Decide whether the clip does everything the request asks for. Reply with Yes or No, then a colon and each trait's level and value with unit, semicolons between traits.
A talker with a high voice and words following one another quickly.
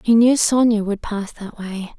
Yes: high, 220 Hz; fast, 210 wpm